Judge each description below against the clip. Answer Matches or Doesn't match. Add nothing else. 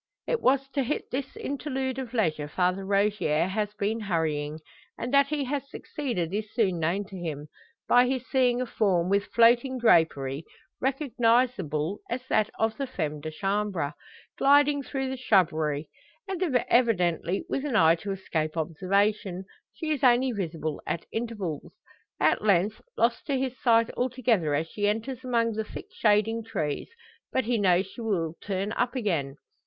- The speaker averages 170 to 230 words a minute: Doesn't match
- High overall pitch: Matches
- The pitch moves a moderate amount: Doesn't match